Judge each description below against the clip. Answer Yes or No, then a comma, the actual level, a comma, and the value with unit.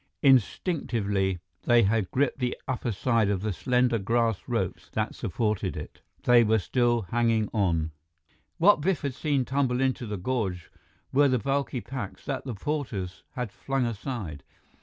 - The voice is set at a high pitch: No, low, 120 Hz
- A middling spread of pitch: Yes, average, 4.4 semitones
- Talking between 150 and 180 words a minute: Yes, average, 155 wpm